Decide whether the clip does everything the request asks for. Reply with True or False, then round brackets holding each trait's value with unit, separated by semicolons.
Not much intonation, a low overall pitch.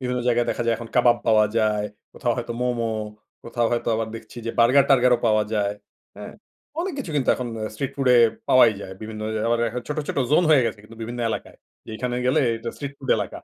True (2.2 semitones; 120 Hz)